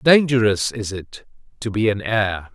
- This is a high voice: No, low, 110 Hz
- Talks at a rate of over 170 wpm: No, average, 165 wpm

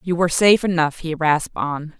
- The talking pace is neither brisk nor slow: No, fast, 210 wpm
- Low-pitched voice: No, medium, 165 Hz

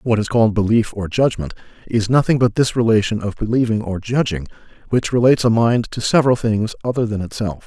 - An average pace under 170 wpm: No, average, 195 wpm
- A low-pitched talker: Yes, low, 110 Hz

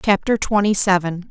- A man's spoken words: No, female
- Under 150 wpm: Yes, average, 140 wpm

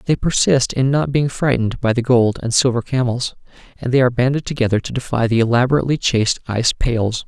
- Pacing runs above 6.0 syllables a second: Yes, 6.2 syllables/s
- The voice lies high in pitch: No, low, 125 Hz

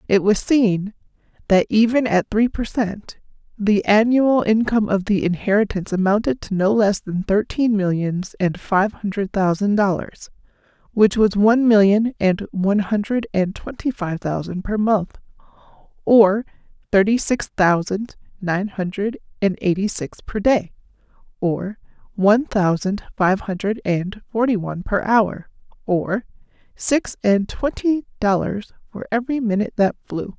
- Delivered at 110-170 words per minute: Yes, average, 140 wpm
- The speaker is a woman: Yes, female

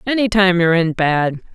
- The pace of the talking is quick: No, average, 195 wpm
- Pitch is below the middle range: No, medium, 185 Hz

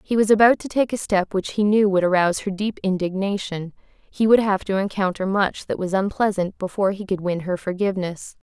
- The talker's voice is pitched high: Yes, high, 195 Hz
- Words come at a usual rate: No, fast, 215 wpm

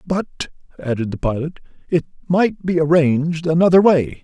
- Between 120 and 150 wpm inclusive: Yes, average, 140 wpm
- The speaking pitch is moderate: Yes, medium, 160 Hz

